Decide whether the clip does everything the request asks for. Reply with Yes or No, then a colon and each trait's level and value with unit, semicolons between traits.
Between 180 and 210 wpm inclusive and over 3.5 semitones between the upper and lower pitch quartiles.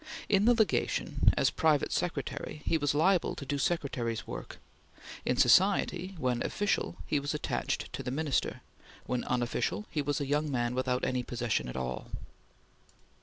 No: average, 160 wpm; average, 4.7 semitones